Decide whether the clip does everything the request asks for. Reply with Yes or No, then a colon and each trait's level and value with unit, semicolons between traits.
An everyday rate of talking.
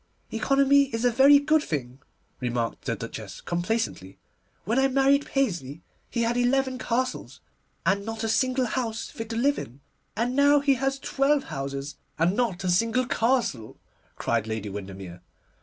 Yes: average, 155 wpm